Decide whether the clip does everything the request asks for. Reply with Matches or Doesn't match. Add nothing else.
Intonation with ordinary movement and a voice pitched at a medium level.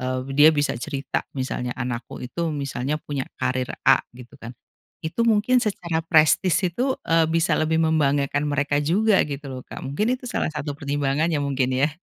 Matches